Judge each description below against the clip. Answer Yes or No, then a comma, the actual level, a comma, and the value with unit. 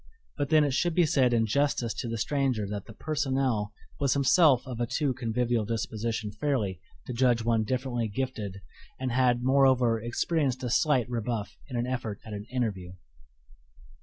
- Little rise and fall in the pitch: No, average, 3.1 semitones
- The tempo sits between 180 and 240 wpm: No, average, 170 wpm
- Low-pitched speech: Yes, low, 120 Hz